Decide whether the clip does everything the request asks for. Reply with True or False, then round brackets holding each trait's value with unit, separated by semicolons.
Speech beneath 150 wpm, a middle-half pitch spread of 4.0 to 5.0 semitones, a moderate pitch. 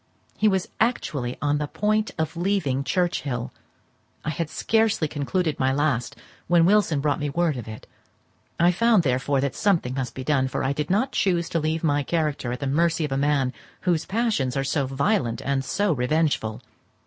False (185 wpm; 4.7 semitones; 150 Hz)